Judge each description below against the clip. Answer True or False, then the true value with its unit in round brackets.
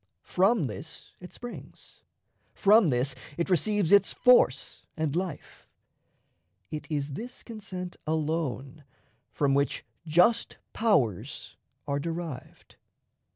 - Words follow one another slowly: True (105 wpm)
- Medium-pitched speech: True (165 Hz)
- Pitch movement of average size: False (6.0 semitones)